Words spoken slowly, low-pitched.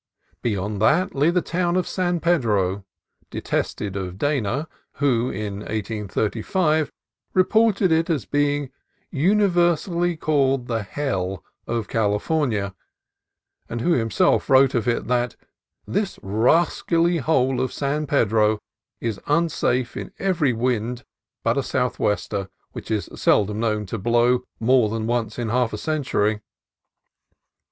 Yes: slow, 125 wpm; low, 125 Hz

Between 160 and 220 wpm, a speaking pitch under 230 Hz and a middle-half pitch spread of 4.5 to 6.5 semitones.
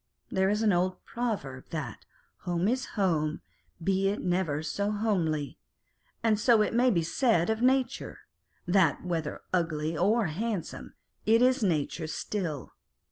No: average, 150 wpm; high, 190 Hz; wide, 5.4 semitones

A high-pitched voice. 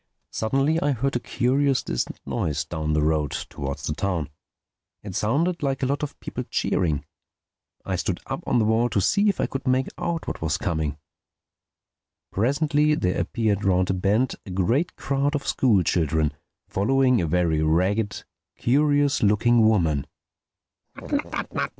No: low, 110 Hz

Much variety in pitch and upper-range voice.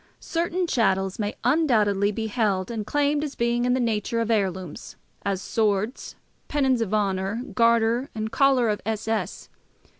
No: average, 3.4 semitones; high, 225 Hz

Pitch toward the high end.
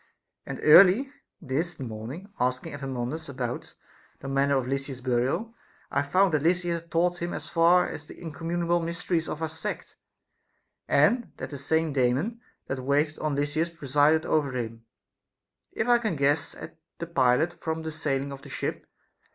No: medium, 155 Hz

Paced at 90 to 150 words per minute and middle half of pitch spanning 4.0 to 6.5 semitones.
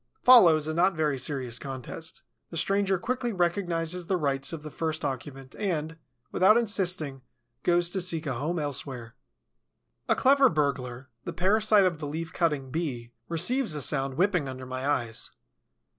No: average, 160 wpm; average, 5.1 semitones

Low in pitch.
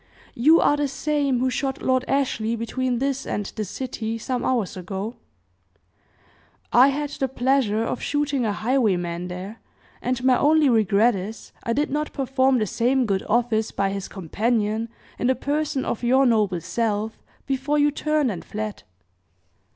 No: high, 245 Hz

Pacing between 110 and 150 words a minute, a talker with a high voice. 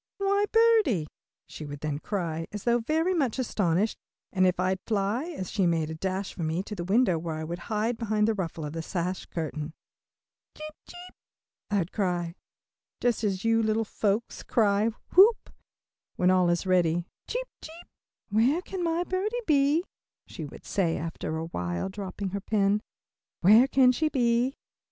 No: average, 170 wpm; high, 205 Hz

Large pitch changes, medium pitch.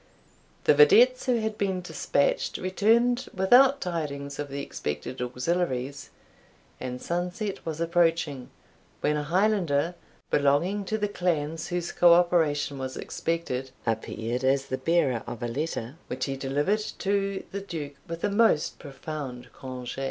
Yes: wide, 5.8 semitones; medium, 165 Hz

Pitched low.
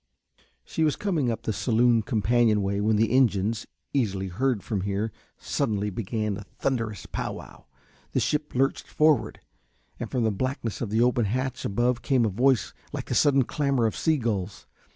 Yes: low, 115 Hz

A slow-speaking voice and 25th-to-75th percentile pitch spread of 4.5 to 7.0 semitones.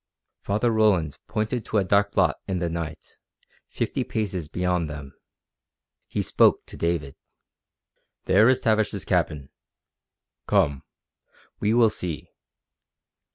Yes: slow, 115 wpm; average, 5.1 semitones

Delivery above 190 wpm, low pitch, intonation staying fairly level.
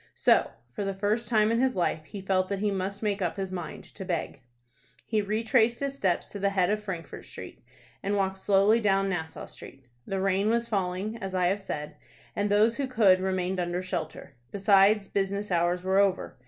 No: average, 200 wpm; high, 195 Hz; narrow, 2.1 semitones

